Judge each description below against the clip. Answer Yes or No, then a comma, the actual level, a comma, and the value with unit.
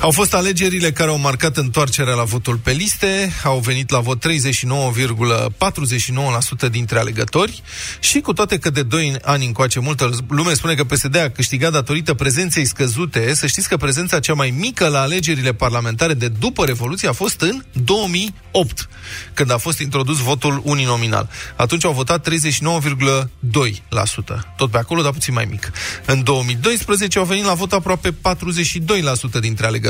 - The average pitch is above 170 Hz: No, medium, 140 Hz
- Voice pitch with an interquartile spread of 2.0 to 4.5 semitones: No, average, 5.2 semitones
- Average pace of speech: Yes, average, 160 wpm